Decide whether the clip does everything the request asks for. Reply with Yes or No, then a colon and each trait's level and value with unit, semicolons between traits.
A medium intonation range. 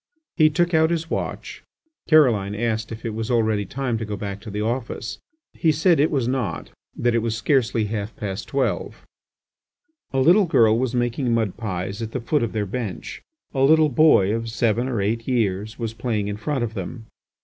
Yes: average, 3.8 semitones